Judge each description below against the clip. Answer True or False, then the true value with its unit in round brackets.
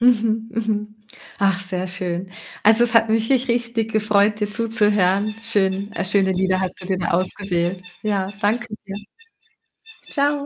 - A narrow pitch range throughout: False (3.0 semitones)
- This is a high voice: True (210 Hz)